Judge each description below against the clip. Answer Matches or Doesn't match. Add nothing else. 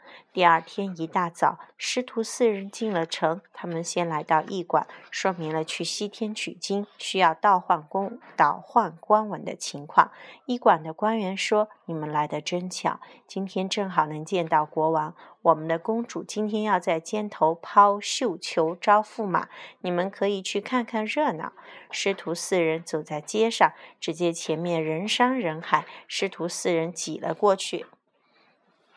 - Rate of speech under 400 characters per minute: Matches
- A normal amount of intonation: Matches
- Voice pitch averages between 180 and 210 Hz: Matches